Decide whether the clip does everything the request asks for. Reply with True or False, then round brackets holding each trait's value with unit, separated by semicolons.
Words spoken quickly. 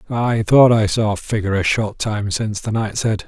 True (240 wpm)